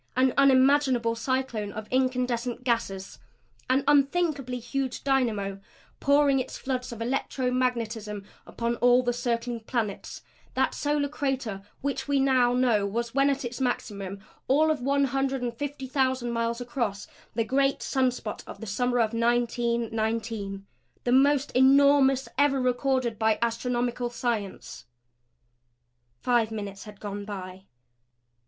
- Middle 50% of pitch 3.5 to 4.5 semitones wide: No, average, 2.9 semitones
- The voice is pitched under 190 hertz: No, high, 245 Hz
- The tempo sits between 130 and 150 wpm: Yes, slow, 135 wpm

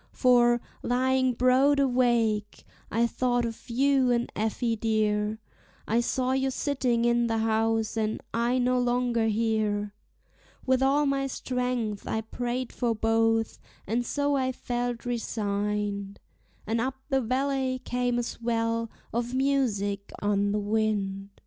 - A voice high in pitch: Yes, high, 235 Hz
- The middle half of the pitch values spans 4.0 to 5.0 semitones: No, narrow, 2.6 semitones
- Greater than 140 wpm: No, slow, 135 wpm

